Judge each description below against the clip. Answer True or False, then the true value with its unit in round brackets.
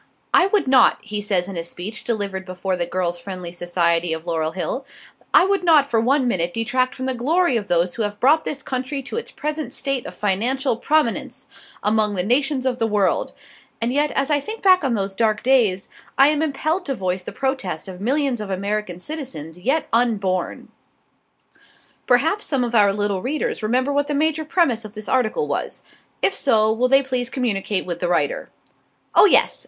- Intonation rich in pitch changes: True (6.3 semitones)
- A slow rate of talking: False (195 wpm)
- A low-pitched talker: False (235 Hz)